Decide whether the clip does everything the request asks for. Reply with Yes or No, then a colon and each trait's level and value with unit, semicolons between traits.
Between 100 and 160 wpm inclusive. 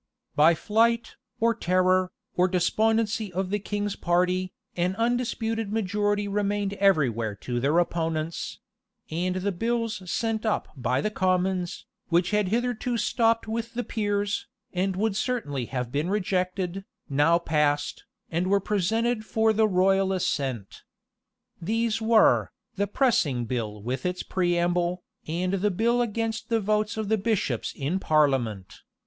Yes: average, 140 wpm